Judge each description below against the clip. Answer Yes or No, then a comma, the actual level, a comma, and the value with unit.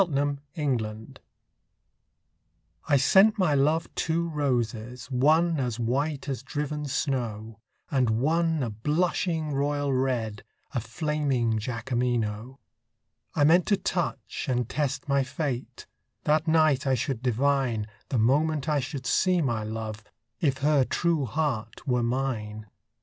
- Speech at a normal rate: No, slow, 130 wpm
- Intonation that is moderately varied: Yes, average, 4.1 semitones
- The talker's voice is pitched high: No, low, 135 Hz